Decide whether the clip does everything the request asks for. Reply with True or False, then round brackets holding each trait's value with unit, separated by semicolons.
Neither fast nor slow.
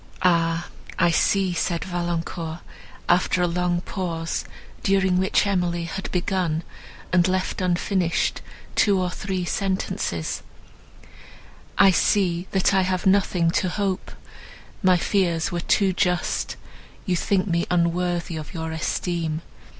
False (125 wpm)